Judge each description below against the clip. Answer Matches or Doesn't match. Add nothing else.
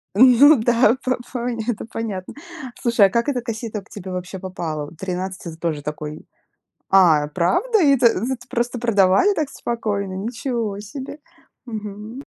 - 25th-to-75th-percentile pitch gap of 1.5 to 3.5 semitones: Doesn't match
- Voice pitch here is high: Matches